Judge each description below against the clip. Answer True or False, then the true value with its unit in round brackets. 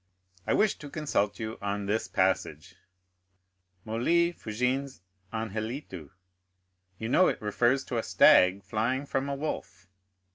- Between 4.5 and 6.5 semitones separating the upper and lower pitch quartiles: True (5.2 semitones)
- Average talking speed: False (130 wpm)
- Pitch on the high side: False (115 Hz)